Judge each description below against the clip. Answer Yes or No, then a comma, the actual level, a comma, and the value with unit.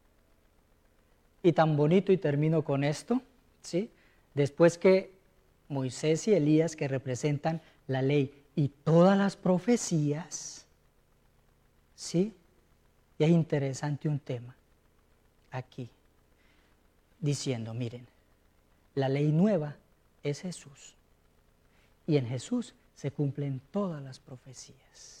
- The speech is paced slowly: Yes, slow, 100 wpm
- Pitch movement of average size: Yes, average, 4.4 semitones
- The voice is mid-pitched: Yes, medium, 145 Hz